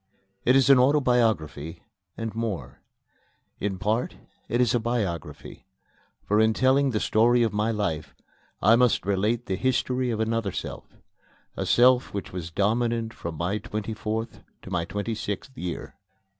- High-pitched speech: No, low, 110 Hz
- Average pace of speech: Yes, average, 155 wpm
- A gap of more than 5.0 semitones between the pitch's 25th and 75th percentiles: No, average, 3.4 semitones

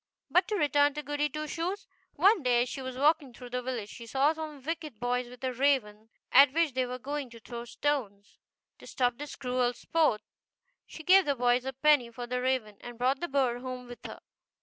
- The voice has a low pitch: No, very high, 260 Hz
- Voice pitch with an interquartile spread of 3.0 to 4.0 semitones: Yes, average, 3.3 semitones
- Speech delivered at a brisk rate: Yes, fast, 215 wpm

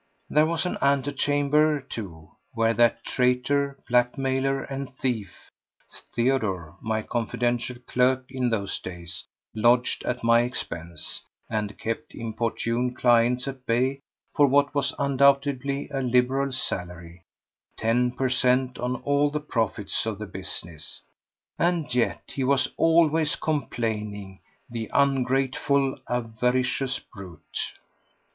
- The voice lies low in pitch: Yes, low, 125 Hz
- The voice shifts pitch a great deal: No, average, 3.4 semitones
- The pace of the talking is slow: Yes, slow, 110 wpm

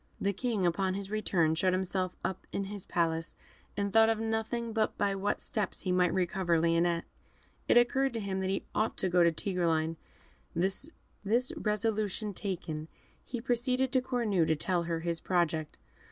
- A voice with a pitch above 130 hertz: Yes, high, 190 Hz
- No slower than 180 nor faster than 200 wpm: No, average, 170 wpm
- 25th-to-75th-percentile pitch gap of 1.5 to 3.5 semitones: No, average, 4.3 semitones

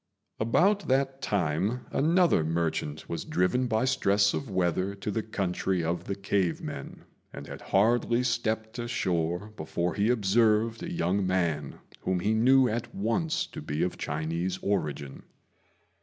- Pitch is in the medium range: No, low, 100 Hz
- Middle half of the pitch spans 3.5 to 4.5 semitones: No, average, 5.3 semitones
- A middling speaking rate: Yes, average, 145 wpm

